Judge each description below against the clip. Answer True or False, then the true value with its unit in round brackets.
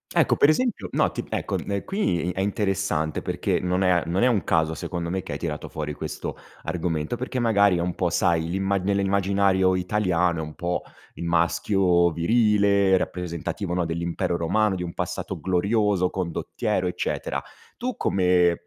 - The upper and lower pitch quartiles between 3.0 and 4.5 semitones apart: False (2.6 semitones)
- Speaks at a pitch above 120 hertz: False (90 Hz)